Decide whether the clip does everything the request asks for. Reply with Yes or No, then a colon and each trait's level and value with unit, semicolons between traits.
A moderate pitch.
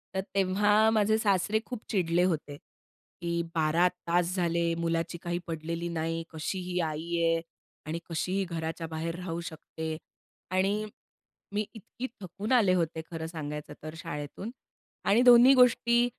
Yes: medium, 175 Hz